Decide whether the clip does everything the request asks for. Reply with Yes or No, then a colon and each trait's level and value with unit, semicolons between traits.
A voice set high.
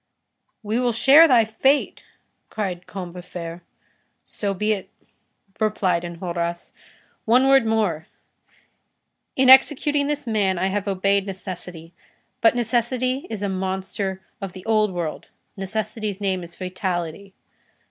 Yes: high, 200 Hz